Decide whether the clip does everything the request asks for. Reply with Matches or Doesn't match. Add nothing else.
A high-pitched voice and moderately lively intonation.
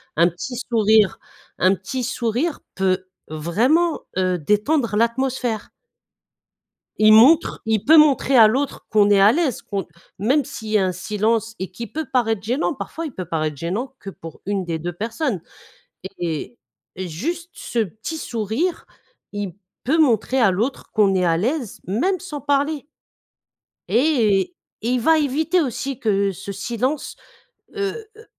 Doesn't match